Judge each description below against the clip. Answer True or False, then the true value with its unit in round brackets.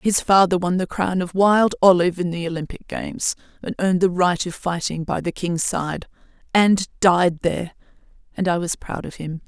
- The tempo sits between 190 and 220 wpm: True (195 wpm)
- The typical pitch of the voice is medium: True (180 Hz)